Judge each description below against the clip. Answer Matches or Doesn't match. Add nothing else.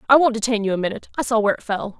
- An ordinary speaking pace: Doesn't match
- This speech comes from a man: Doesn't match